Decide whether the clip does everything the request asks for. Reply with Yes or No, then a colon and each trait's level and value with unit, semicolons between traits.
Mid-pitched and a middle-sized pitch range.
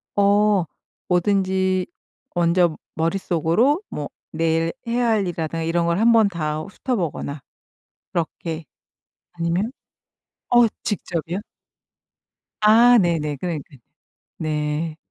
Yes: medium, 175 Hz; average, 4.0 semitones